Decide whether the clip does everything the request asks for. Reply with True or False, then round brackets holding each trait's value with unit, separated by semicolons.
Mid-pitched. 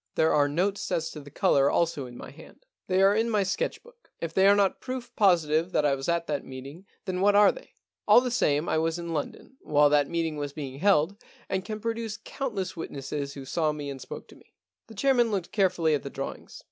True (170 Hz)